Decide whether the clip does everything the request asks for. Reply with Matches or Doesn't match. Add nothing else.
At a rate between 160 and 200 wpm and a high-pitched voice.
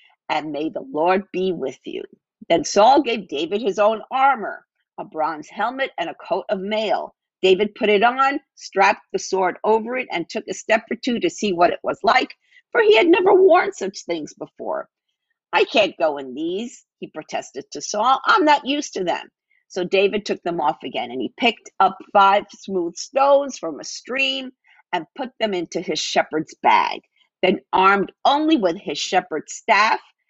Matches